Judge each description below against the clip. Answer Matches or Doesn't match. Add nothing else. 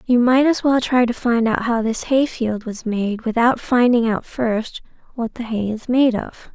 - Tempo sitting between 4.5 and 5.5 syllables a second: Doesn't match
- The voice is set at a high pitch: Matches